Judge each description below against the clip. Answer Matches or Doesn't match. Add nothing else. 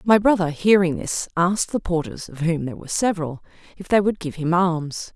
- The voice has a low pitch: Doesn't match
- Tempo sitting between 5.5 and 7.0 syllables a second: Matches